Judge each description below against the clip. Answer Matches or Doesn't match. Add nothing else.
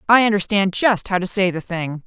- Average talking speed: Doesn't match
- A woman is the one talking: Matches